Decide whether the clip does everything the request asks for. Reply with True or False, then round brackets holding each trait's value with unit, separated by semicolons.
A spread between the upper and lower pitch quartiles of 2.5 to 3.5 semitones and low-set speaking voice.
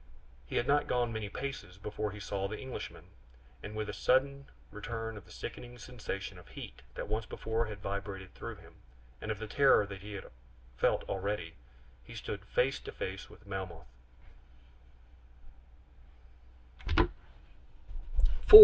True (3.0 semitones; 105 Hz)